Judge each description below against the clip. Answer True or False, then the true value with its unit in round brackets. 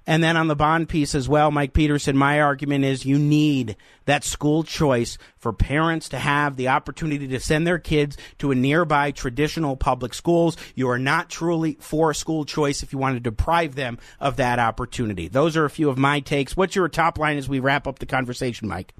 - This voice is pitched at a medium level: True (145 Hz)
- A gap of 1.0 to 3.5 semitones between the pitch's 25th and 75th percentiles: True (3.0 semitones)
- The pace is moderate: False (215 wpm)